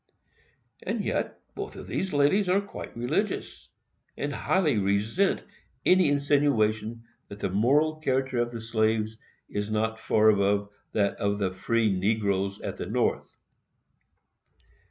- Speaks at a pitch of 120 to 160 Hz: No, low, 110 Hz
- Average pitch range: No, wide, 5.7 semitones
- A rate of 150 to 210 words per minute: No, slow, 135 wpm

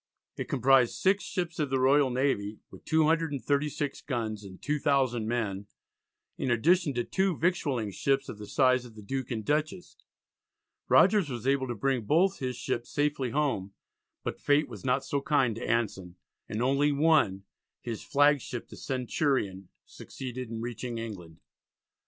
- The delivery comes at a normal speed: Yes, average, 155 wpm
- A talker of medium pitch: No, low, 130 Hz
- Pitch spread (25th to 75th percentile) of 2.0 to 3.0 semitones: No, average, 4.2 semitones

